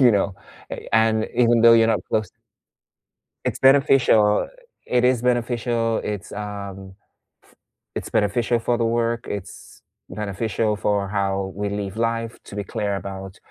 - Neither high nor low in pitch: No, low, 110 Hz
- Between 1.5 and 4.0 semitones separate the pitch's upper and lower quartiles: Yes, average, 2.7 semitones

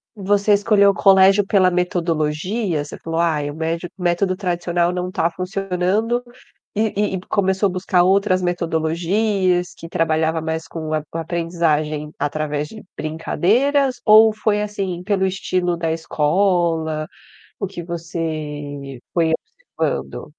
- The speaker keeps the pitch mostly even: No, average, 3.4 semitones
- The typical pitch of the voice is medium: Yes, medium, 175 Hz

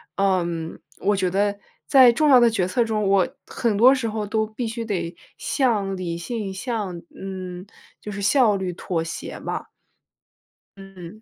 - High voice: Yes, high, 200 Hz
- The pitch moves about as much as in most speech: Yes, average, 3.6 semitones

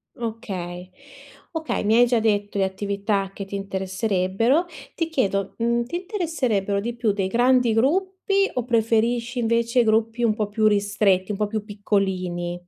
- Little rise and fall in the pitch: No, average, 3.3 semitones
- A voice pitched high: Yes, high, 220 Hz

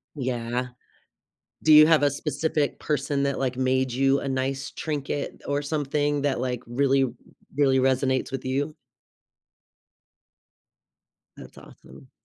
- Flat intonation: Yes, narrow, 1.7 semitones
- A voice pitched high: No, low, 135 Hz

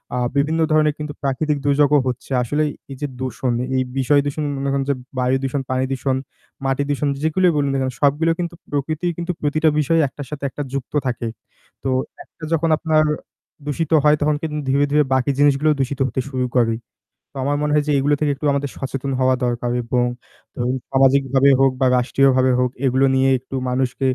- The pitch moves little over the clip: Yes, narrow, 2.3 semitones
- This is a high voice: No, medium, 140 Hz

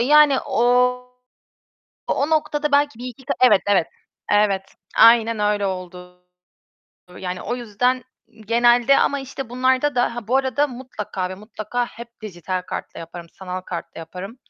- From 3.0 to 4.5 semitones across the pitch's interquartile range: No, average, 5.1 semitones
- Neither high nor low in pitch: No, high, 235 Hz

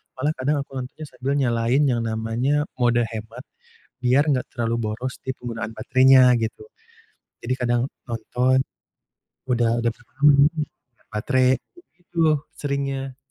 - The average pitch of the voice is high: No, low, 130 Hz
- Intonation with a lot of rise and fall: No, average, 2.9 semitones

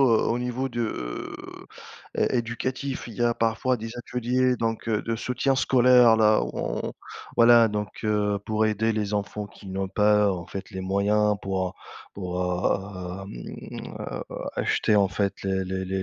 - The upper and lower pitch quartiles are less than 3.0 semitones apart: No, average, 3.4 semitones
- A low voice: Yes, low, 105 Hz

